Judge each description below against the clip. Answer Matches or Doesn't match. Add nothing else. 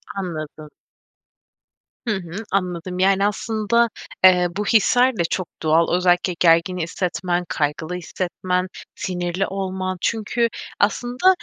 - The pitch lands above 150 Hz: Matches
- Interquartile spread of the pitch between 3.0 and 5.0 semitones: Doesn't match